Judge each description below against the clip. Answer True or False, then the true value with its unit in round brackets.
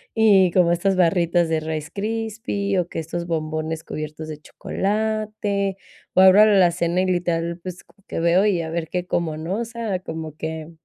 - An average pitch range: True (3.5 semitones)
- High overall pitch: False (175 Hz)